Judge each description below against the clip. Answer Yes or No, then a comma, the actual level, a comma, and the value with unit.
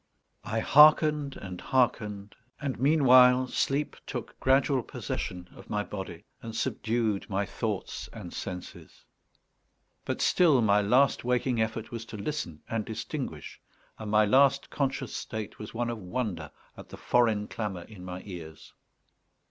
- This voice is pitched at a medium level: No, low, 110 Hz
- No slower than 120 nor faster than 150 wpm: Yes, average, 140 wpm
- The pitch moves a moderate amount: Yes, average, 4.3 semitones